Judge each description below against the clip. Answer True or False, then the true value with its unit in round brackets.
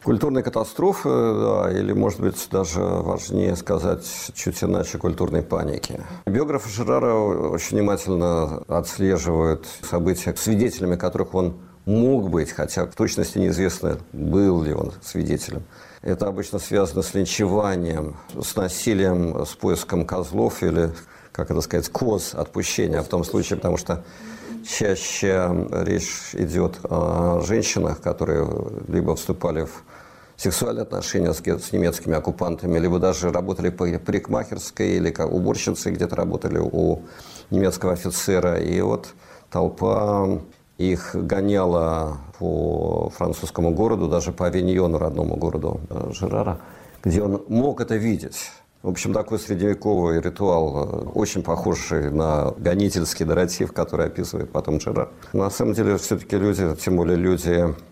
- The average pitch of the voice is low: True (90 Hz)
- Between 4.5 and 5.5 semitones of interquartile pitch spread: False (2.9 semitones)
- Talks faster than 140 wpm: False (125 wpm)